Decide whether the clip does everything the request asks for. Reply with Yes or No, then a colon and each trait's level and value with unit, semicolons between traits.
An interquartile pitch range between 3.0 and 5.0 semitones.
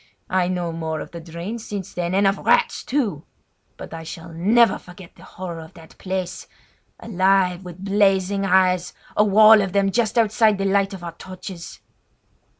No: narrow, 2.6 semitones